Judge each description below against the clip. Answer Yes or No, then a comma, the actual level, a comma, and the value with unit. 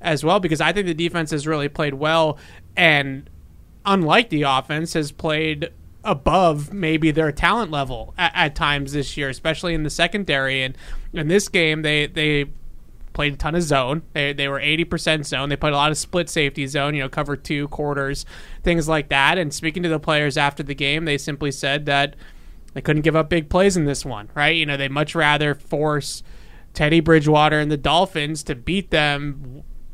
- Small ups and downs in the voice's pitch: Yes, narrow, 2.2 semitones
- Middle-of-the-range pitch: Yes, medium, 150 Hz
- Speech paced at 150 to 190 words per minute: No, average, 200 wpm